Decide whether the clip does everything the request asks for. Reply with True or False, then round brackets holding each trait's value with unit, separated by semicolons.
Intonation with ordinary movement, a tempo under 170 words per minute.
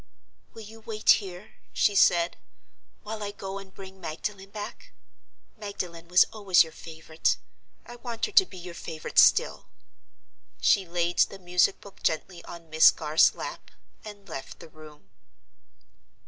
True (3.6 semitones; 145 wpm)